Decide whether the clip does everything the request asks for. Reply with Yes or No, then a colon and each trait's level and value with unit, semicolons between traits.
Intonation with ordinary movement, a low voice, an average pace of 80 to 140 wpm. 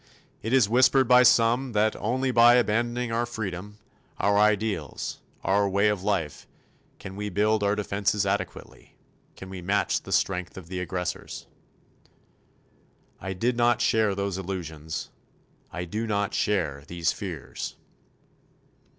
Yes: average, 3.4 semitones; low, 105 Hz; slow, 135 wpm